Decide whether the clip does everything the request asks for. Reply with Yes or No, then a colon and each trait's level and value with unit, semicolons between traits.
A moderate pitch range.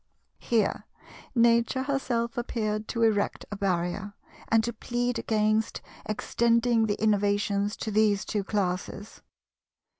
No: narrow, 2.3 semitones